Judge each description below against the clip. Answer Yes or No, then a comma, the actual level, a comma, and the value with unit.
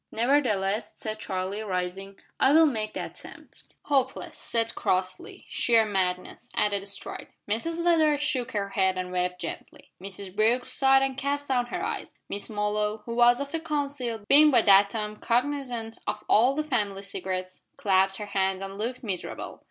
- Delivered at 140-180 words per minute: Yes, average, 165 wpm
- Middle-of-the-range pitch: No, high, 215 Hz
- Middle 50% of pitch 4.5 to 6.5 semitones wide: Yes, average, 5.2 semitones